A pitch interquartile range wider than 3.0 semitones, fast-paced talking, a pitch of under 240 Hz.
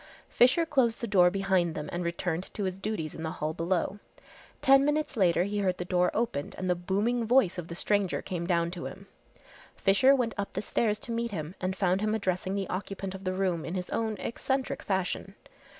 Yes: average, 3.6 semitones; fast, 215 wpm; high, 190 Hz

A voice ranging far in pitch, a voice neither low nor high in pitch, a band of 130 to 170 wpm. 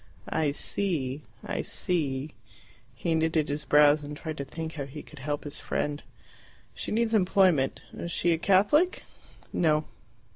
No: average, 3.2 semitones; medium, 155 Hz; average, 150 wpm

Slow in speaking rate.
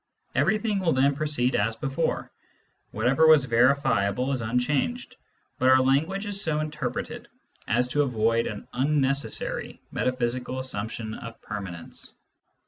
Yes: slow, 125 wpm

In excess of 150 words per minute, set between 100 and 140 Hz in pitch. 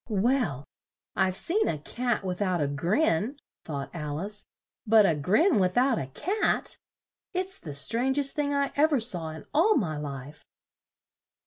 No: average, 170 wpm; high, 205 Hz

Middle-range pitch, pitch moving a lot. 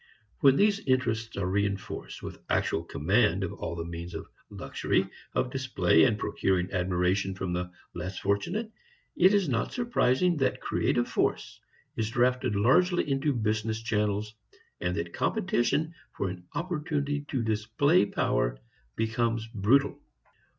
No: low, 110 Hz; wide, 6.3 semitones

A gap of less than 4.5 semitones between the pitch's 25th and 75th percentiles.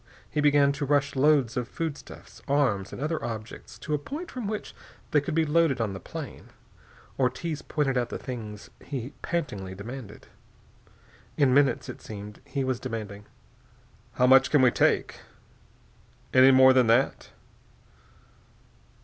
Yes: average, 4.1 semitones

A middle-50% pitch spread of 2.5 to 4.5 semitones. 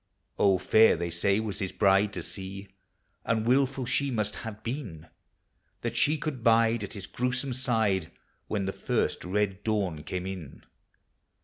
Yes: average, 3.6 semitones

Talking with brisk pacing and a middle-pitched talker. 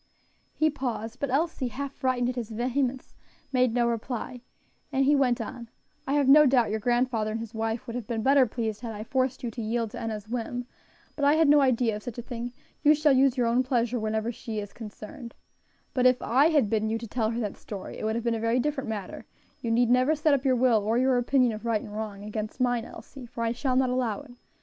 No: fast, 245 wpm; high, 240 Hz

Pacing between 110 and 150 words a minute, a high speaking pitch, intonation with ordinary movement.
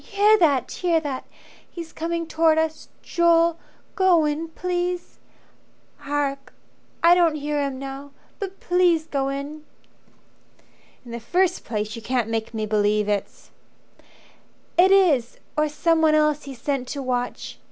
Yes: average, 140 wpm; very high, 300 Hz; average, 4.3 semitones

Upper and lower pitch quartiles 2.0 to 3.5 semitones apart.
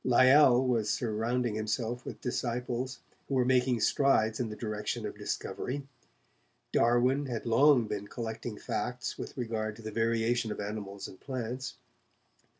Yes: narrow, 2.5 semitones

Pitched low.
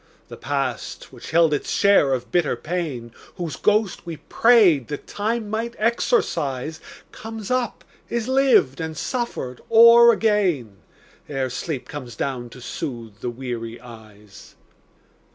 No: medium, 155 Hz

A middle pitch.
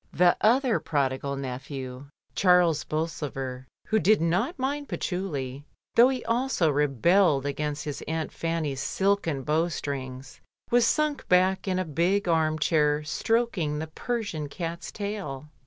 Yes: medium, 160 Hz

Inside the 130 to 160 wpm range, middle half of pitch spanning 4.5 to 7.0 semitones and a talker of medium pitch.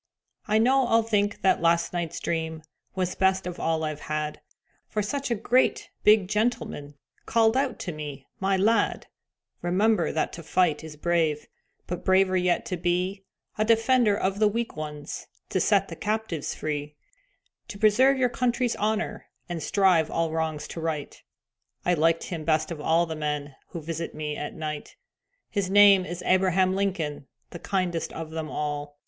No: average, 170 wpm; average, 4.8 semitones; medium, 180 Hz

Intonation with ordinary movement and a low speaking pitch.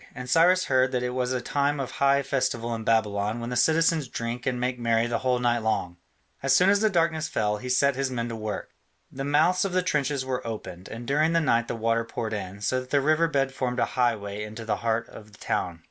Yes: average, 3.6 semitones; low, 125 Hz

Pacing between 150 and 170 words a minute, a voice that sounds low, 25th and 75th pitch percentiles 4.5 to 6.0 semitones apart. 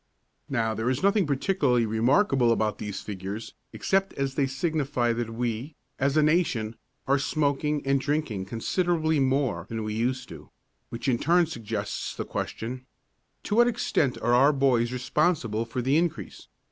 Yes: average, 160 wpm; low, 130 Hz; average, 4.8 semitones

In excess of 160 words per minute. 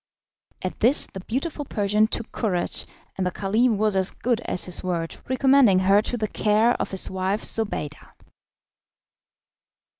No: average, 150 wpm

